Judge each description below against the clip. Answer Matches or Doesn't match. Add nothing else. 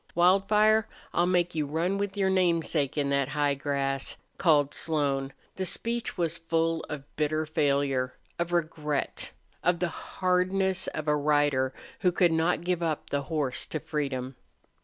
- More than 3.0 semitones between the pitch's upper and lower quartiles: Matches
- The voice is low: Doesn't match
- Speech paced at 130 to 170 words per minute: Matches